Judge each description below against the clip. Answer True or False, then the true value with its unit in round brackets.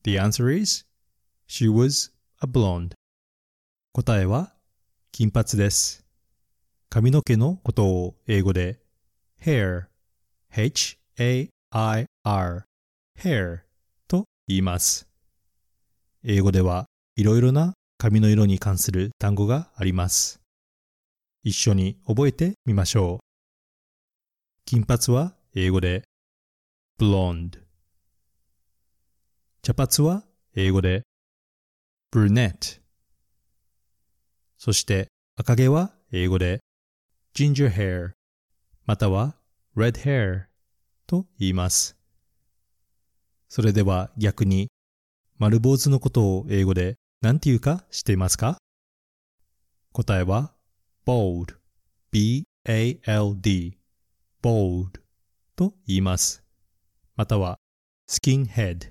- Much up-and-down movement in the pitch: False (4.4 semitones)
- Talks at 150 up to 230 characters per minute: True (215 characters per minute)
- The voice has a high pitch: False (100 Hz)